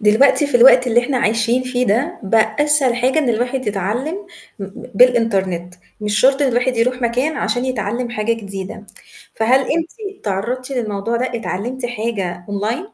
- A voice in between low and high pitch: No, high, 240 Hz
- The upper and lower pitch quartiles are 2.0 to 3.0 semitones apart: No, average, 3.5 semitones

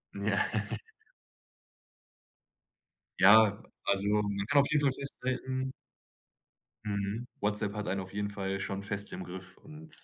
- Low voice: Yes, low, 105 Hz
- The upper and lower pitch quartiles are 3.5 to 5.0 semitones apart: Yes, average, 4.2 semitones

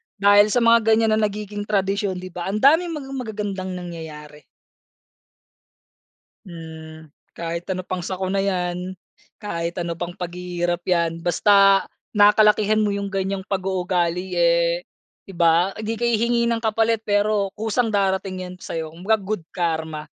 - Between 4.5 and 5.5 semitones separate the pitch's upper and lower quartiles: No, average, 3.3 semitones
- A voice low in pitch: No, high, 190 Hz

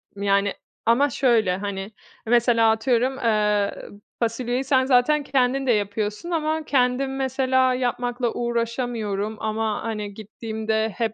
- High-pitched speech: Yes, high, 235 Hz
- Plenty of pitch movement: No, average, 3.2 semitones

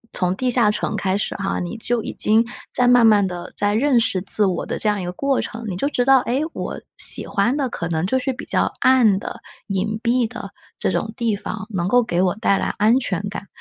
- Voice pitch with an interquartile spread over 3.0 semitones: Yes, average, 4.1 semitones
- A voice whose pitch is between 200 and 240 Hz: Yes, high, 215 Hz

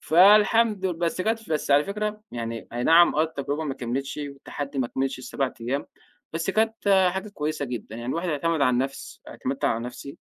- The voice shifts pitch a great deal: Yes, wide, 5.9 semitones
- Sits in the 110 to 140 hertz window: No, medium, 150 Hz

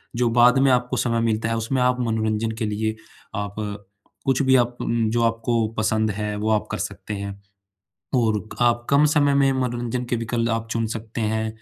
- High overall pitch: No, low, 115 Hz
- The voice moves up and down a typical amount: No, narrow, 2.1 semitones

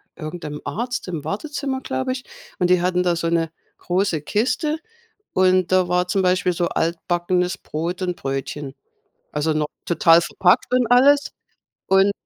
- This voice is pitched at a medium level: Yes, medium, 180 Hz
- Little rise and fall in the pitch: No, average, 3.0 semitones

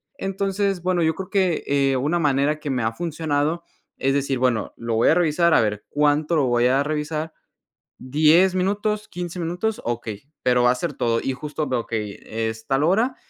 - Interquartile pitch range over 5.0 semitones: Yes, wide, 5.4 semitones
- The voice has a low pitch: No, medium, 150 Hz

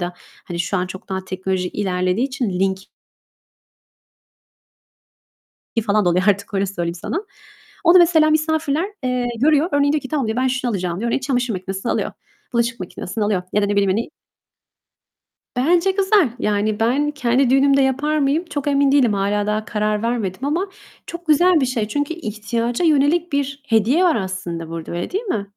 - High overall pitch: Yes, high, 235 Hz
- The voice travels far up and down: Yes, wide, 6.4 semitones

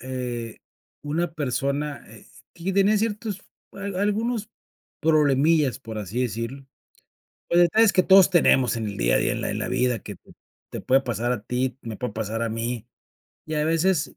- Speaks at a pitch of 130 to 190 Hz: Yes, low, 135 Hz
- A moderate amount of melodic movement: No, wide, 6.9 semitones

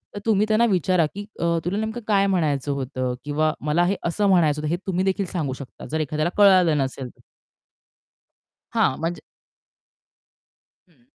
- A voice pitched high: No, medium, 170 Hz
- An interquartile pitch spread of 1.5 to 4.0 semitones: No, average, 4.8 semitones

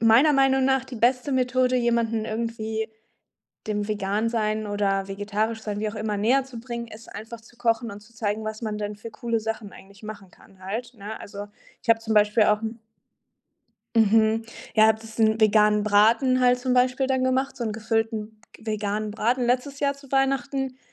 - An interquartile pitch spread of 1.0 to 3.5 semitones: Yes, average, 2.7 semitones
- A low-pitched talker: No, high, 225 Hz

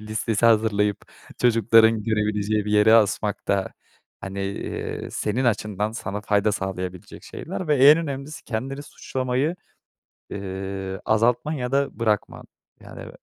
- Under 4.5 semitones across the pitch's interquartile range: Yes, average, 3.4 semitones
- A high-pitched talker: No, low, 110 Hz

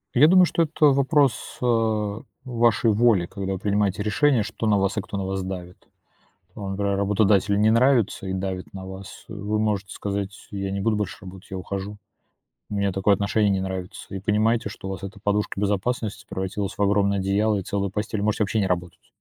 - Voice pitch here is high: No, low, 100 Hz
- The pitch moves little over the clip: Yes, narrow, 1.9 semitones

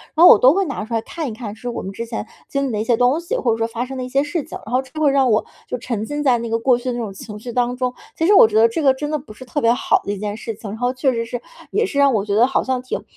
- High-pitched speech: Yes, high, 245 Hz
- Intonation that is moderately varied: Yes, average, 3.3 semitones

